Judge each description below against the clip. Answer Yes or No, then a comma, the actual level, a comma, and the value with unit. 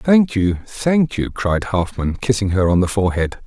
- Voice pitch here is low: Yes, low, 105 Hz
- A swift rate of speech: No, average, 190 wpm